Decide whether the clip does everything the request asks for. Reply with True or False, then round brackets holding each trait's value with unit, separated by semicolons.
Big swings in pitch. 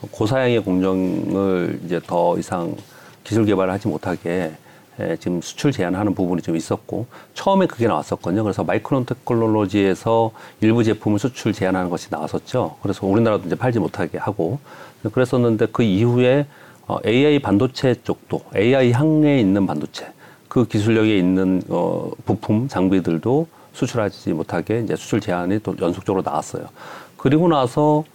False (5.0 semitones)